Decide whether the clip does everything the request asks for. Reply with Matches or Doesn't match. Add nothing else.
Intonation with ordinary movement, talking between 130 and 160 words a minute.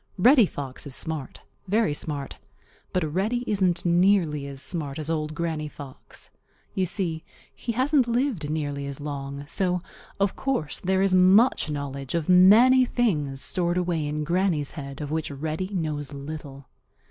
Matches